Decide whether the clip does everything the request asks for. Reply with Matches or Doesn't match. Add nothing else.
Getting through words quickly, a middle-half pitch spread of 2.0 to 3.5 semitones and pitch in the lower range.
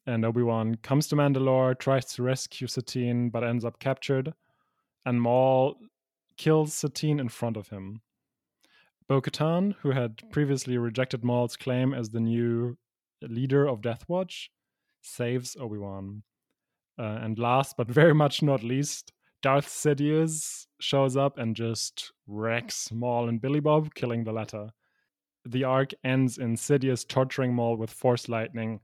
Doesn't match